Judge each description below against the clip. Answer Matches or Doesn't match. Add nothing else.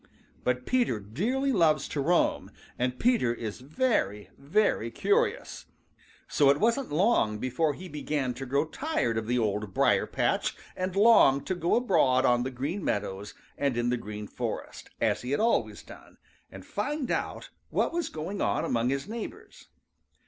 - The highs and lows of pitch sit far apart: Matches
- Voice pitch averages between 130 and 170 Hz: Matches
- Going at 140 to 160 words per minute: Doesn't match